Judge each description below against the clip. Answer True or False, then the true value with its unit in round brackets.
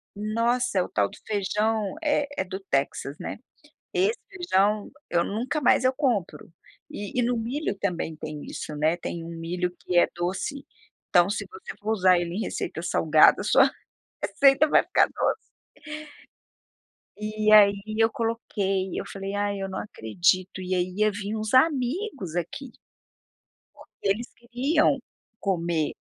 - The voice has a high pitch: True (205 Hz)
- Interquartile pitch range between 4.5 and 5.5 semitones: True (5.0 semitones)